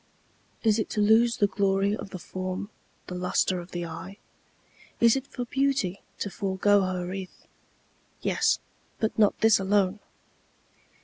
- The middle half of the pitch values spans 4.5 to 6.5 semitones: No, average, 2.9 semitones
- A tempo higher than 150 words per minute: No, average, 145 wpm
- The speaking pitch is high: Yes, high, 200 Hz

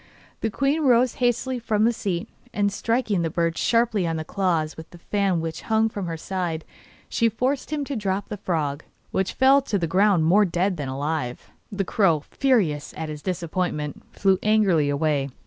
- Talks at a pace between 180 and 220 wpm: Yes, average, 185 wpm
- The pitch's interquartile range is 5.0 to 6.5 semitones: Yes, wide, 5.5 semitones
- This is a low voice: No, high, 190 Hz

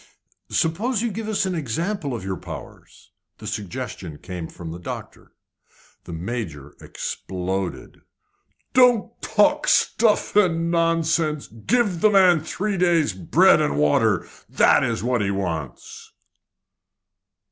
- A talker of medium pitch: Yes, medium, 155 Hz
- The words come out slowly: Yes, slow, 125 wpm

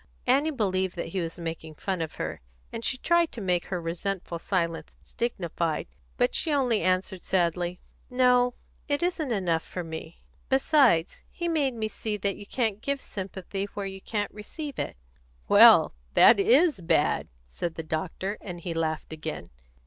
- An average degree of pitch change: No, wide, 6.5 semitones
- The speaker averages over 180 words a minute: No, average, 170 wpm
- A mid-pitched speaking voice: No, high, 195 Hz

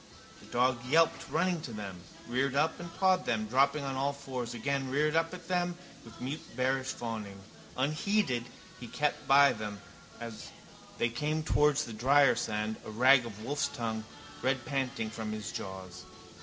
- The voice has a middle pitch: No, low, 130 Hz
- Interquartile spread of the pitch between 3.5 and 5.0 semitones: Yes, average, 4.4 semitones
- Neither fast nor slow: Yes, average, 165 wpm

